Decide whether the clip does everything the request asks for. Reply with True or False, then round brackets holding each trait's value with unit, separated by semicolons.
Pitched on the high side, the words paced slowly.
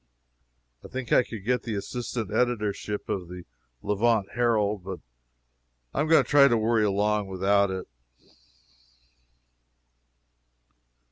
False (105 Hz; 125 wpm)